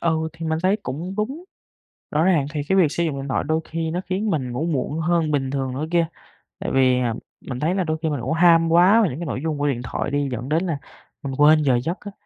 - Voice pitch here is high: No, medium, 160 Hz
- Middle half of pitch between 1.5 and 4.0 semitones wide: Yes, average, 3.7 semitones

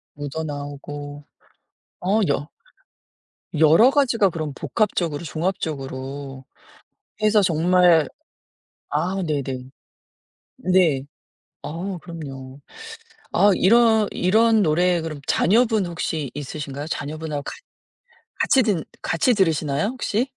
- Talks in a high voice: No, medium, 165 Hz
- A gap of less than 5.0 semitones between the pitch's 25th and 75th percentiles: No, average, 5.3 semitones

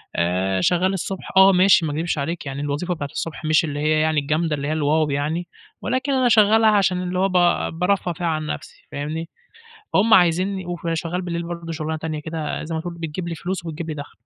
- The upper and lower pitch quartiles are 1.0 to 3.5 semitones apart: Yes, average, 2.9 semitones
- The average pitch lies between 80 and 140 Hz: No, medium, 165 Hz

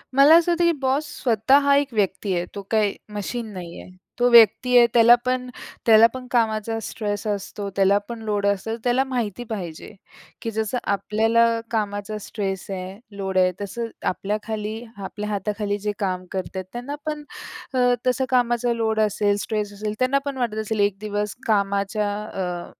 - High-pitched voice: Yes, high, 215 Hz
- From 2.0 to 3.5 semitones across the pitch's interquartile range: Yes, average, 3.1 semitones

